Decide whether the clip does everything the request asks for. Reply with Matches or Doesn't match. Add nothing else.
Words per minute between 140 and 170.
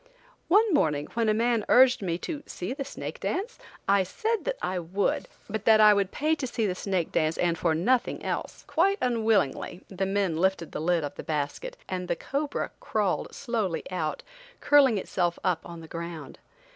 Doesn't match